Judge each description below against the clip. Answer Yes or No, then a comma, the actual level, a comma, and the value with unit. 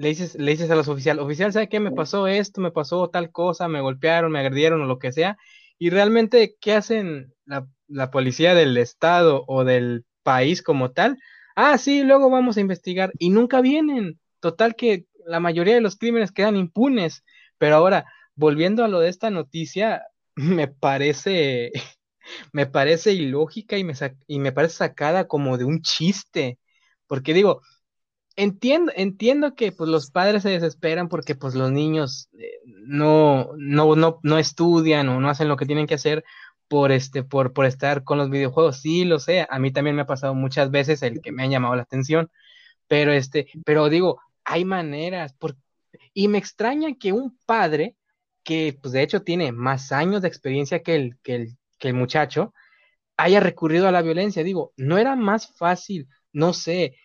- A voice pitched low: No, medium, 165 Hz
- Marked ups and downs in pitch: Yes, wide, 5.9 semitones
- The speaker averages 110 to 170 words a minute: No, average, 185 wpm